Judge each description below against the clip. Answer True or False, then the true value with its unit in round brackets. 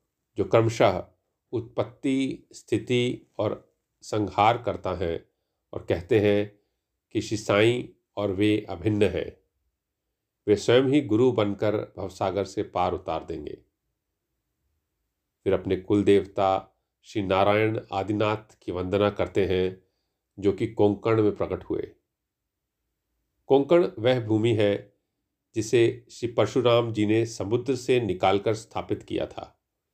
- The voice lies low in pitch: True (105 Hz)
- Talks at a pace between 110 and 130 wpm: True (120 wpm)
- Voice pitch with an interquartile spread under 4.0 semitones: True (2.8 semitones)